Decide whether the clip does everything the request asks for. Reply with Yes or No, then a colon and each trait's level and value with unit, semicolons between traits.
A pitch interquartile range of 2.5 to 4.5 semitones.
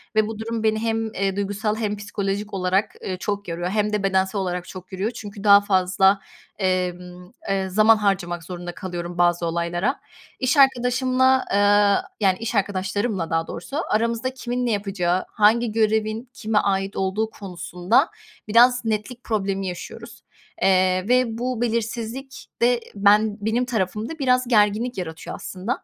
Yes: average, 3.4 semitones